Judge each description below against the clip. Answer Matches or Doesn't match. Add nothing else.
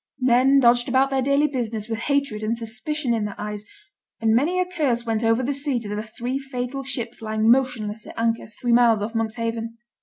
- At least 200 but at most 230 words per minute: Matches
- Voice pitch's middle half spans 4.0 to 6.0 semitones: Doesn't match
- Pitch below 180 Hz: Doesn't match